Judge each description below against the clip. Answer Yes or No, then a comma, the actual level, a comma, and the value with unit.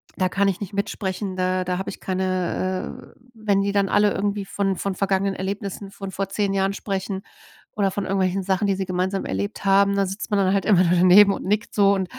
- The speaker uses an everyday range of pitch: No, narrow, 1.2 semitones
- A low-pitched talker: No, high, 195 Hz